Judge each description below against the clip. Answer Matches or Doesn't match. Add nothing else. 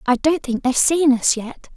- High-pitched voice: Matches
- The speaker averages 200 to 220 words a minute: Doesn't match